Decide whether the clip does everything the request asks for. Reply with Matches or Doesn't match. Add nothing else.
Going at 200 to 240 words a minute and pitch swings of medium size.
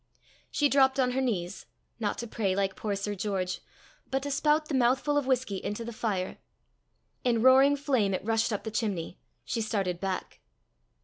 Doesn't match